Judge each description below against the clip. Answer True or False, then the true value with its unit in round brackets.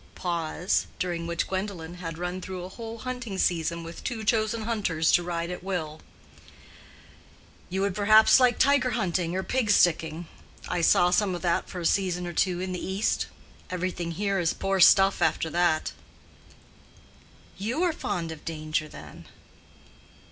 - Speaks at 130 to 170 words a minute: True (160 wpm)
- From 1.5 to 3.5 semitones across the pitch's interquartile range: True (3.2 semitones)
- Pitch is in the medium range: True (180 Hz)